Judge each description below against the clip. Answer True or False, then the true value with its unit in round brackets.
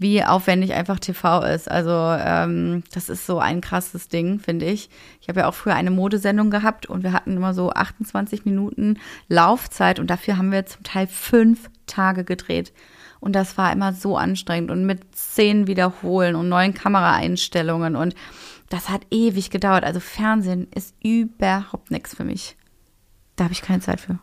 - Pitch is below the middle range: False (190 Hz)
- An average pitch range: False (2.1 semitones)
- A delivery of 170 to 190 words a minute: True (175 wpm)